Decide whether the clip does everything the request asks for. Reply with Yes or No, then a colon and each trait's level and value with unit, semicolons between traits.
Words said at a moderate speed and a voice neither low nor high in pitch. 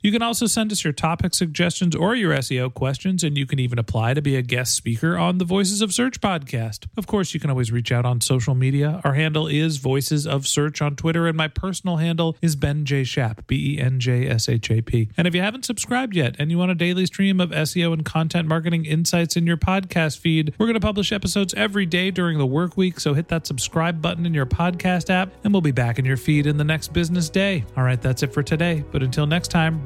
No: fast, 235 wpm; medium, 160 Hz